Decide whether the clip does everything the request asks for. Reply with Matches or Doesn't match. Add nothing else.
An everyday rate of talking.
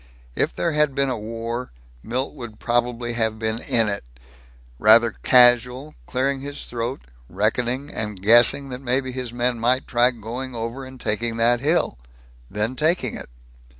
Matches